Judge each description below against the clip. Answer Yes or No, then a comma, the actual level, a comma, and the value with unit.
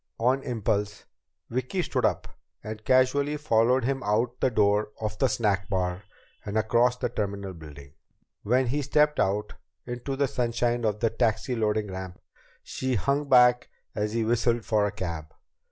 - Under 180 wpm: Yes, average, 160 wpm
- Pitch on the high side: No, low, 115 Hz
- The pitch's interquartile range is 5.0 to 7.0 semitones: No, average, 3.5 semitones